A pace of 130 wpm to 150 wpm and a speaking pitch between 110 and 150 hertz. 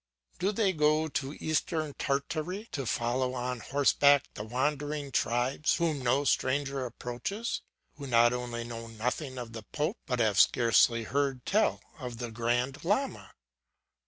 Yes: average, 145 wpm; low, 135 Hz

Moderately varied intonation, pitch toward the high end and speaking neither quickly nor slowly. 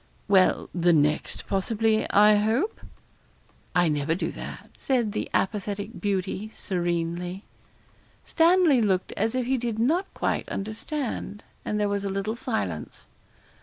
No: average, 3.6 semitones; high, 205 Hz; slow, 130 wpm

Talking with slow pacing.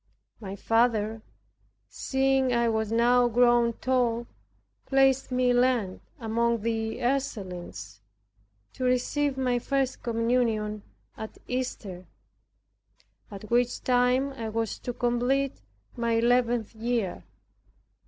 Yes: slow, 105 wpm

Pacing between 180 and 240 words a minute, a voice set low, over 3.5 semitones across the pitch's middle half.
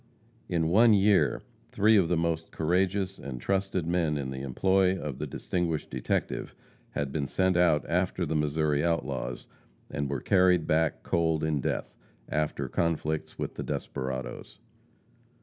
No: average, 150 wpm; very low, 80 Hz; average, 3.9 semitones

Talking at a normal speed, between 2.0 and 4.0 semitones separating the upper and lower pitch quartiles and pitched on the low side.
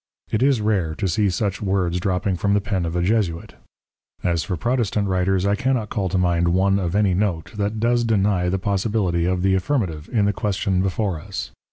No: fast, 210 wpm; average, 2.7 semitones; very low, 95 Hz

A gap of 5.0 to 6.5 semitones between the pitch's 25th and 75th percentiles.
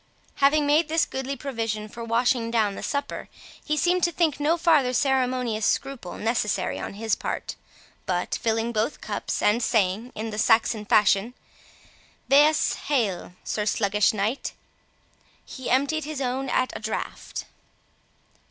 No: average, 4.6 semitones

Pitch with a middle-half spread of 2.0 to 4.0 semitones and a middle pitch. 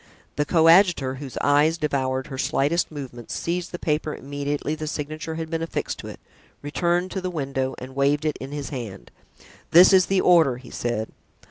Yes: average, 3.6 semitones; medium, 150 Hz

